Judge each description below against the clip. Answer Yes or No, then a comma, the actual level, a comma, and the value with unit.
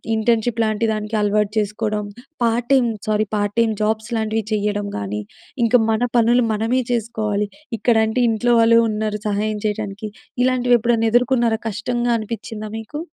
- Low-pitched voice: No, high, 220 Hz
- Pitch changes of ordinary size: No, narrow, 1.9 semitones